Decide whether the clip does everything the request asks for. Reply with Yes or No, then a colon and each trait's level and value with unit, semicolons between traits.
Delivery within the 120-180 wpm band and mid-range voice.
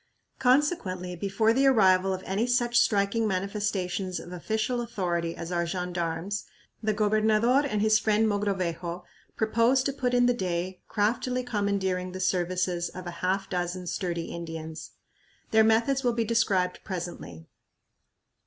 No: average, 140 wpm; high, 195 Hz